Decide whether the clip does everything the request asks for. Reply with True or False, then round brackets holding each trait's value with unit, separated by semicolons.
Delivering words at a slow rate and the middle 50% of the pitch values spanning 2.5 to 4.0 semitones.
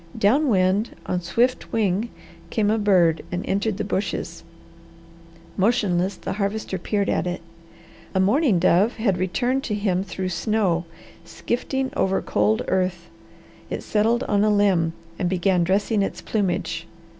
False (145 wpm; 3.2 semitones)